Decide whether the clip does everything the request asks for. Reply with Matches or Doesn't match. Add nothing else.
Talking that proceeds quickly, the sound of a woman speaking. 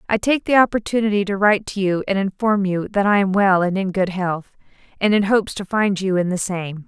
Matches